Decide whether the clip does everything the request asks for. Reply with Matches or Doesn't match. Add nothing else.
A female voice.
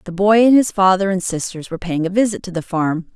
Matches